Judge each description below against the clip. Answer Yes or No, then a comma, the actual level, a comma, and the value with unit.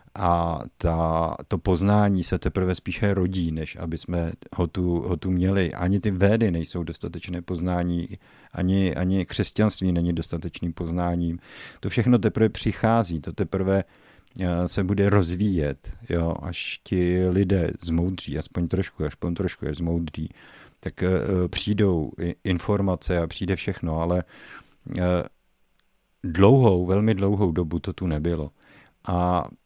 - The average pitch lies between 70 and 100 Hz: Yes, very low, 90 Hz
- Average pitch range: No, narrow, 2.3 semitones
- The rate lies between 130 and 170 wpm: Yes, average, 135 wpm